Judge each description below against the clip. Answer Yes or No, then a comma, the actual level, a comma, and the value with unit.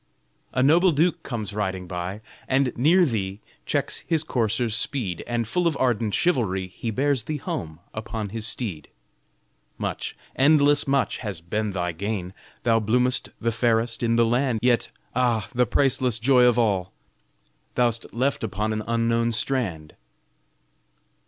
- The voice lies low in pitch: Yes, low, 115 Hz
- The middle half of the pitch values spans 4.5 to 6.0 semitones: No, average, 3.6 semitones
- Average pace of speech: Yes, average, 145 wpm